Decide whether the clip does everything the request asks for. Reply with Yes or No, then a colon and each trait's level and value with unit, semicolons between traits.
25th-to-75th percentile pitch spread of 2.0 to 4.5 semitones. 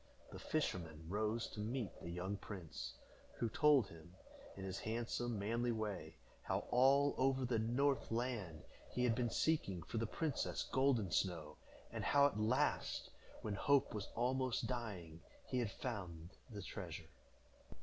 No: average, 5.1 semitones